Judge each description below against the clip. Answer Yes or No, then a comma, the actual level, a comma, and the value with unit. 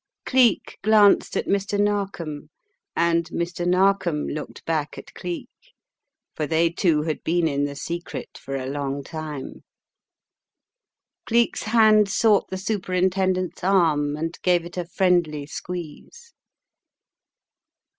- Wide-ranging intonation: No, average, 4.2 semitones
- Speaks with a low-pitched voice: No, medium, 175 Hz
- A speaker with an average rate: No, slow, 120 wpm